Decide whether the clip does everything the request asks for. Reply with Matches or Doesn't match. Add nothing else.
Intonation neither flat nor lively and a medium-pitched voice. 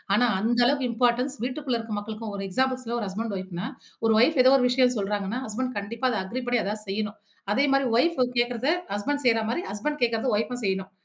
Doesn't match